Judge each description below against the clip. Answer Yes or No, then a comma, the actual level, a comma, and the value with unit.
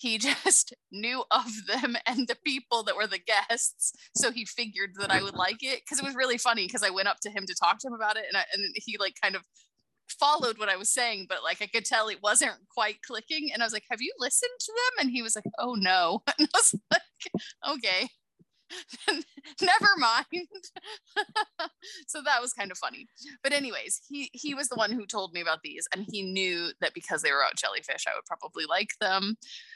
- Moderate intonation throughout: No, wide, 6.3 semitones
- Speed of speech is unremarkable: No, fast, 225 wpm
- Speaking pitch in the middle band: No, high, 245 Hz